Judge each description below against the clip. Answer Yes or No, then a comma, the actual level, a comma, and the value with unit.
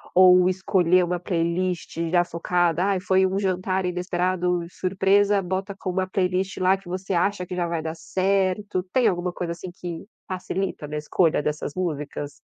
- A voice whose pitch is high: No, medium, 180 Hz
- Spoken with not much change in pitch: Yes, narrow, 1.4 semitones